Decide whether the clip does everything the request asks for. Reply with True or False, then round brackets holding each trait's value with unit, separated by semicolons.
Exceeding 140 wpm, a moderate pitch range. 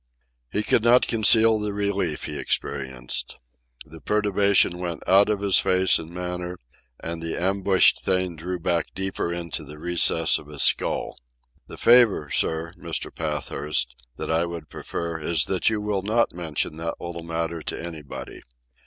True (160 wpm; 3.5 semitones)